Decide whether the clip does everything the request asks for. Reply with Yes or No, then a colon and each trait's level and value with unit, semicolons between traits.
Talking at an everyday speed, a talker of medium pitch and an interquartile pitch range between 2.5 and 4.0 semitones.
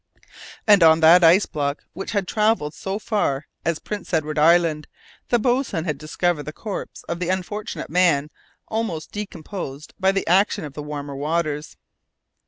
No: average, 160 wpm; medium, 170 Hz; average, 4.4 semitones